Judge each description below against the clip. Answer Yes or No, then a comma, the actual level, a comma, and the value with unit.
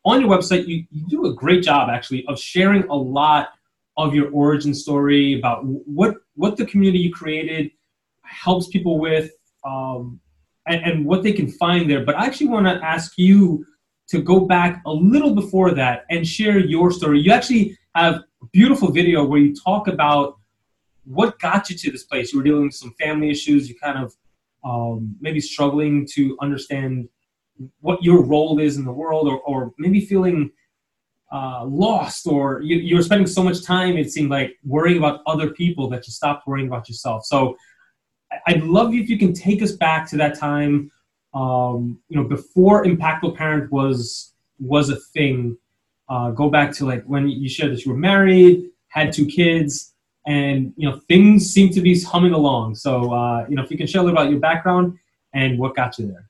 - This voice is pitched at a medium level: Yes, medium, 150 Hz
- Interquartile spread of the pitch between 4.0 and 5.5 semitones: Yes, average, 4.6 semitones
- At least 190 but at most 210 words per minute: Yes, average, 195 wpm